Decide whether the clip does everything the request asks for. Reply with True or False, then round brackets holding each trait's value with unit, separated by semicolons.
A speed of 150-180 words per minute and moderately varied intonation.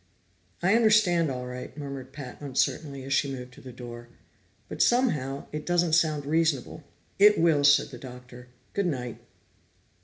True (155 wpm; 4.7 semitones)